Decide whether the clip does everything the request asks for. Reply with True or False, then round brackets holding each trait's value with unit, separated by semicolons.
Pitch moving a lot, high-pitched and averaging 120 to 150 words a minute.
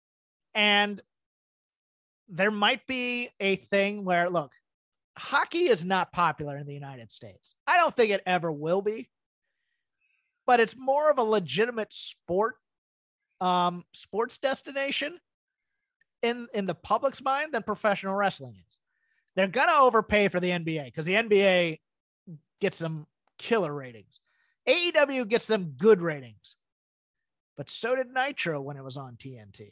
True (7.1 semitones; 205 Hz; 140 wpm)